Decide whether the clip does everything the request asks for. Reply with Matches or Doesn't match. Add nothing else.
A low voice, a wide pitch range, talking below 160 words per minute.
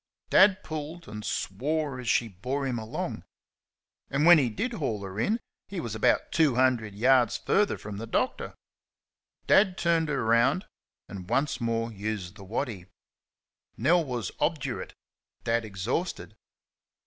Matches